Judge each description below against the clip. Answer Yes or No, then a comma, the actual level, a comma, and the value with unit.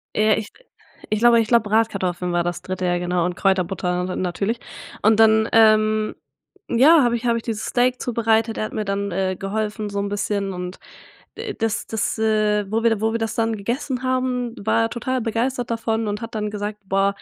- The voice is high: Yes, high, 215 Hz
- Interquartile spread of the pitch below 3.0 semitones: Yes, narrow, 2.5 semitones